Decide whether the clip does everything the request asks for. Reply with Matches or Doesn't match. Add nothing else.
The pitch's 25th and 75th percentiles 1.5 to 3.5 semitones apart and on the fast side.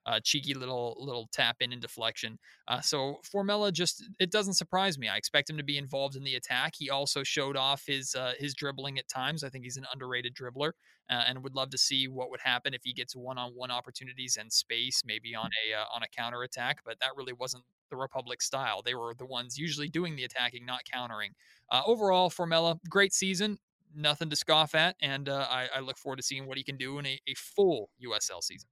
Matches